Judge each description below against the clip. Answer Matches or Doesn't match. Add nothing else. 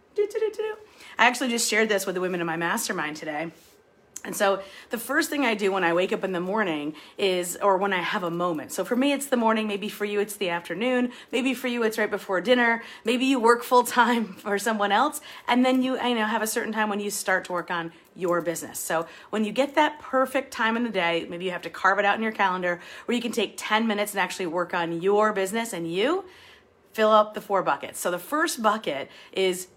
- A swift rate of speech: Matches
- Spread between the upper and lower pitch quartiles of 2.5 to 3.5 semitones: Doesn't match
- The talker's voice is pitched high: Matches